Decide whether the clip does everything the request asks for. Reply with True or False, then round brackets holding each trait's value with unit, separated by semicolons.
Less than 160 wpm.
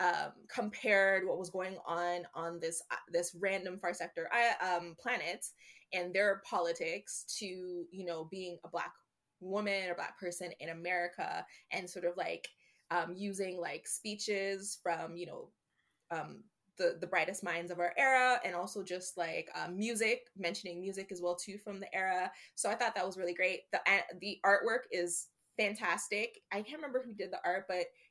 False (180 wpm)